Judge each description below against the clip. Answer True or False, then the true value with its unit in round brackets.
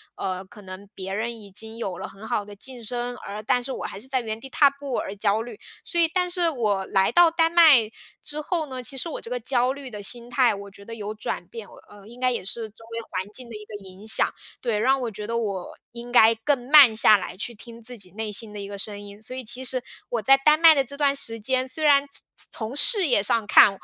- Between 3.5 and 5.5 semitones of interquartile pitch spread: True (4.3 semitones)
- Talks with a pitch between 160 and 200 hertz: False (230 Hz)